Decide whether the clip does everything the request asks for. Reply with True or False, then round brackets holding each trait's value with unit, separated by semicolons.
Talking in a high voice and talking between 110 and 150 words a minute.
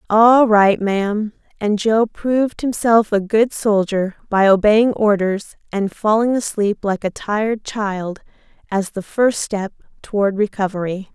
True (210 Hz; 140 wpm)